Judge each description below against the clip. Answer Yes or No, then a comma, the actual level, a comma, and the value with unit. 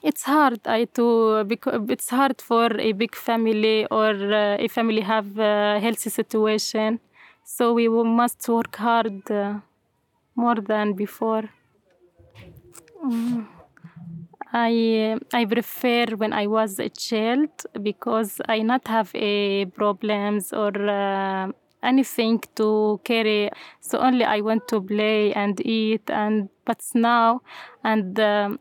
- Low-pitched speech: No, high, 220 Hz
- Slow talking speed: Yes, slow, 130 wpm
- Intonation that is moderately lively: No, narrow, 1.9 semitones